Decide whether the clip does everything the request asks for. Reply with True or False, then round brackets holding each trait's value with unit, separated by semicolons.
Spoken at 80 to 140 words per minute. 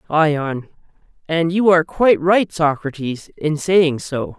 True (135 wpm)